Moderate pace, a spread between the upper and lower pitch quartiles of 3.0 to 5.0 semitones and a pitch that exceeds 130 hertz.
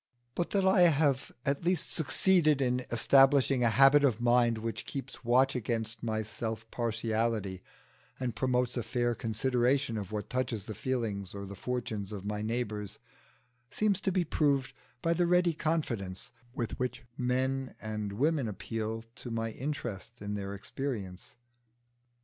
No: average, 150 wpm; average, 3.9 semitones; low, 120 Hz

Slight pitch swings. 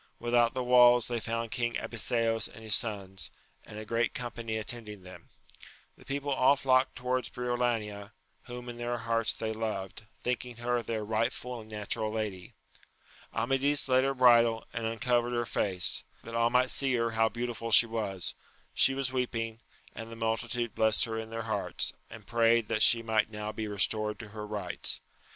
Yes: narrow, 1.9 semitones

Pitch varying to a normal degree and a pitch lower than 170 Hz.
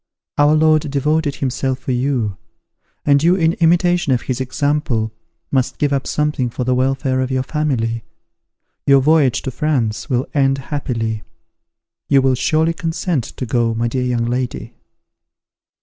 Yes: average, 3.3 semitones; low, 135 Hz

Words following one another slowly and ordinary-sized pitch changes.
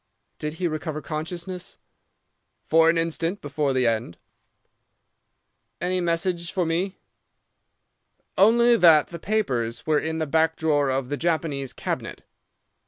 Yes: slow, 125 wpm; average, 3.1 semitones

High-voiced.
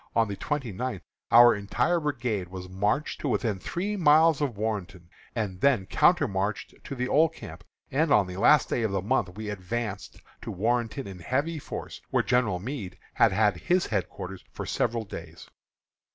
No: low, 110 Hz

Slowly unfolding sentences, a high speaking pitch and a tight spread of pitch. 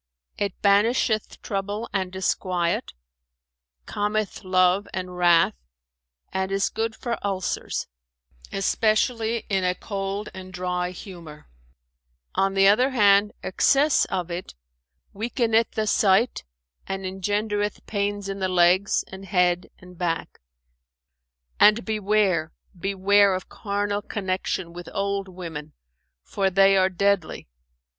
Yes: slow, 115 wpm; high, 195 Hz; narrow, 2.1 semitones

